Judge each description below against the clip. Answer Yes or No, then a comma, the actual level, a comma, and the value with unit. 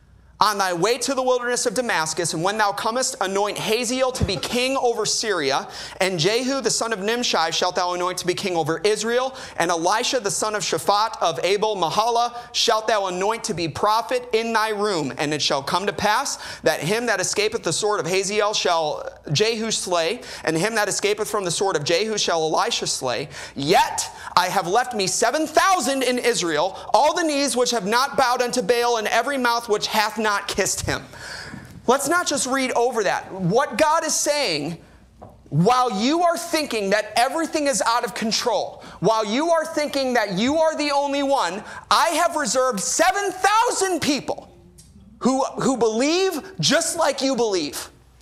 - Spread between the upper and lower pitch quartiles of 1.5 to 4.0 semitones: No, wide, 5.5 semitones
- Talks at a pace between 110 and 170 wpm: No, average, 185 wpm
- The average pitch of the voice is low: No, high, 230 Hz